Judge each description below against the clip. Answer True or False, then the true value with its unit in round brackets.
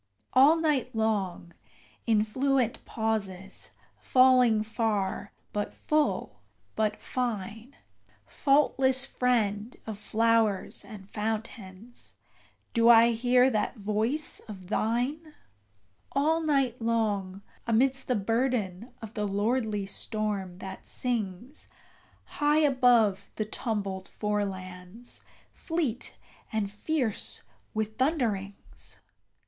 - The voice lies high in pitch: True (225 Hz)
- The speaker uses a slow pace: True (95 wpm)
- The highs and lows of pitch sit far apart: False (3.7 semitones)